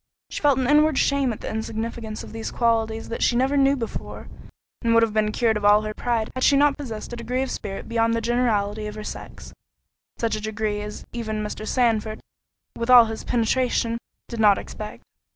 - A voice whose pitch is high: Yes, high, 230 Hz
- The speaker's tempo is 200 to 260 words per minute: Yes, fast, 205 wpm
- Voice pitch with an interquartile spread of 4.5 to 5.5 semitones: No, narrow, 2.4 semitones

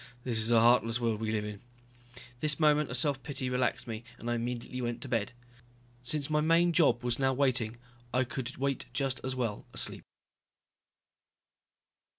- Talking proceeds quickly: No, average, 170 wpm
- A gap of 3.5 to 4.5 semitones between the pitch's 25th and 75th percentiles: No, average, 2.9 semitones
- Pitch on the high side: No, low, 125 Hz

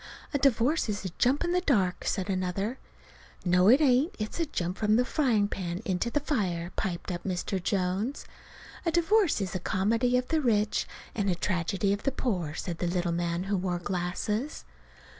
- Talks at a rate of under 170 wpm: No, average, 190 wpm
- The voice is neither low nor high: No, high, 205 Hz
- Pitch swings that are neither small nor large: No, wide, 5.7 semitones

